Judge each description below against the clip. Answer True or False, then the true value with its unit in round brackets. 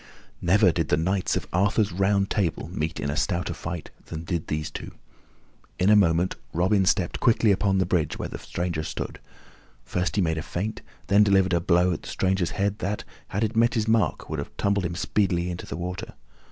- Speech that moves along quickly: True (210 wpm)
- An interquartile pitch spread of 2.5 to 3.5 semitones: True (2.8 semitones)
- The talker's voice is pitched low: True (90 Hz)